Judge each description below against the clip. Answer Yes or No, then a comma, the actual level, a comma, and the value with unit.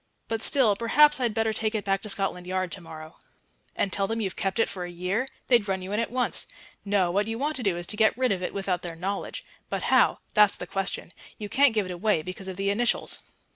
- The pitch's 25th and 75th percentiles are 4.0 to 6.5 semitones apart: No, average, 3.4 semitones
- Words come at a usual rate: No, fast, 250 wpm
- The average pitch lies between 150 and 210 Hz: Yes, high, 200 Hz